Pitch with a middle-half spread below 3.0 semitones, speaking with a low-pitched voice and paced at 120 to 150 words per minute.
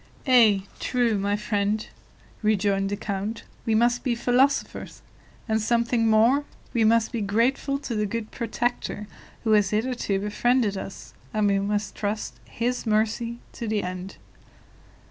No: narrow, 2.6 semitones; high, 220 Hz; average, 145 wpm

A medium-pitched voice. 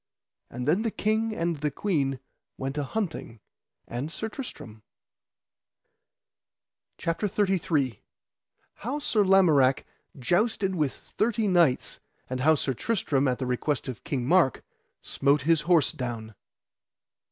Yes: medium, 155 Hz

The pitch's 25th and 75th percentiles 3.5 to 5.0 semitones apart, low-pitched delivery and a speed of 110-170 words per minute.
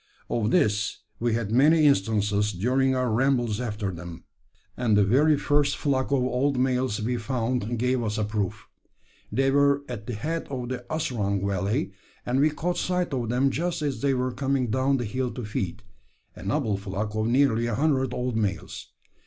No: average, 4.2 semitones; low, 125 Hz; average, 185 wpm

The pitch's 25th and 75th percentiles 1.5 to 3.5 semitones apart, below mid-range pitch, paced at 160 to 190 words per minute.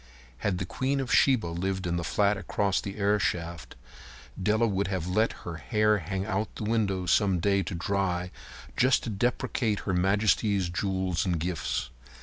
Yes: average, 2.9 semitones; very low, 95 Hz; average, 165 wpm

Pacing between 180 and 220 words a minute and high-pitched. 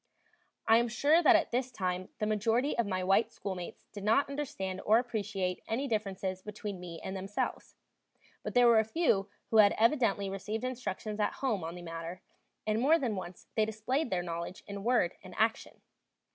Yes: average, 185 wpm; high, 215 Hz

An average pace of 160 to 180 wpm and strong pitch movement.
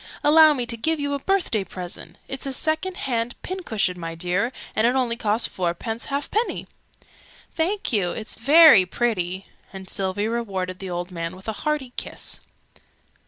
Yes: average, 165 wpm; wide, 7.3 semitones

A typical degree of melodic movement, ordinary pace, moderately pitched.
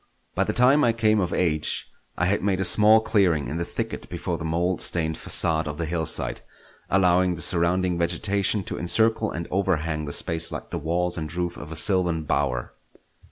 No: average, 3.0 semitones; average, 195 wpm; very low, 85 Hz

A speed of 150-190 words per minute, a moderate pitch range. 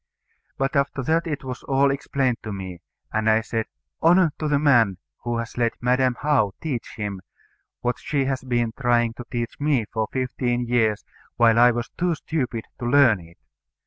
Yes: average, 180 wpm; average, 3.4 semitones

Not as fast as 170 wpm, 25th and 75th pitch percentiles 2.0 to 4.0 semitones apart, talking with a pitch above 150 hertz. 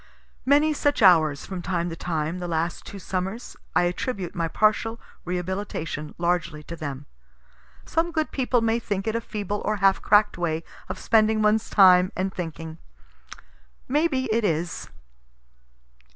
No: average, 150 wpm; average, 4.7 semitones; high, 190 Hz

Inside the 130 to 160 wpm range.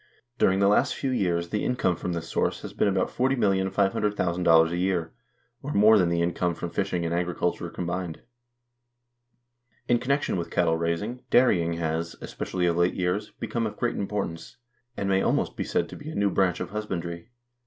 No: average, 185 wpm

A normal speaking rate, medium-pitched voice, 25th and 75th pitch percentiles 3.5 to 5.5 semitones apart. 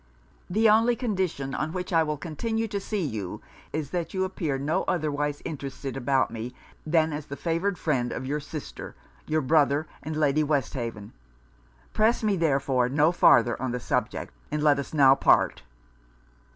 Yes: average, 165 wpm; medium, 150 Hz; average, 4.2 semitones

